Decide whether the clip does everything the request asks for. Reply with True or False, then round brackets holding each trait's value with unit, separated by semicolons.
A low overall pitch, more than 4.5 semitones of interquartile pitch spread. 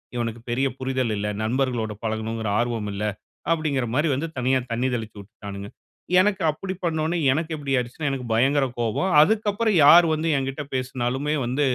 True (130 Hz; 5.0 semitones)